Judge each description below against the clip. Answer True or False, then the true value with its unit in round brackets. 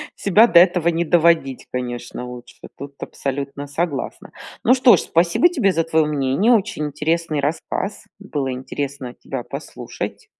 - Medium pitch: True (155 Hz)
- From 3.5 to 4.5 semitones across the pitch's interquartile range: True (4.2 semitones)